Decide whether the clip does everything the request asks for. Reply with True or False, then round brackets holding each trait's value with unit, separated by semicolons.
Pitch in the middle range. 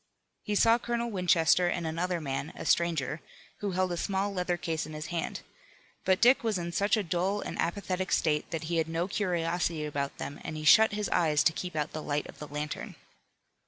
True (175 Hz)